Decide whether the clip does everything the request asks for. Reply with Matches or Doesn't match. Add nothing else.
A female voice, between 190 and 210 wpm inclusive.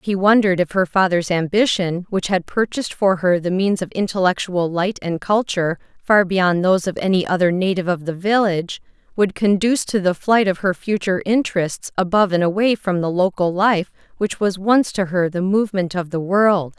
Matches